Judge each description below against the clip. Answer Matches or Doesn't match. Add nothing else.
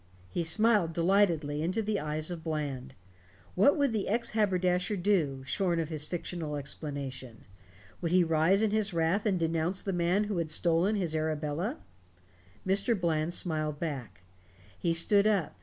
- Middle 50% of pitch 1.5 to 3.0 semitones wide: Doesn't match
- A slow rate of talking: Doesn't match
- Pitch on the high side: Doesn't match